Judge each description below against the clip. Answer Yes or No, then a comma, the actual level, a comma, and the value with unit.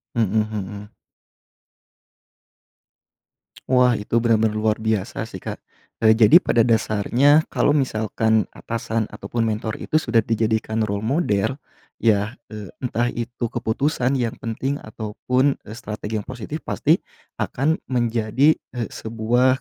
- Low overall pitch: Yes, low, 115 Hz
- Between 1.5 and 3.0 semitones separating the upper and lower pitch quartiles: Yes, narrow, 2.5 semitones